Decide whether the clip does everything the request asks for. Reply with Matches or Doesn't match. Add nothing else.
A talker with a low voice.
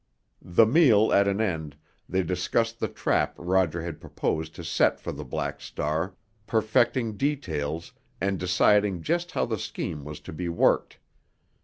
Matches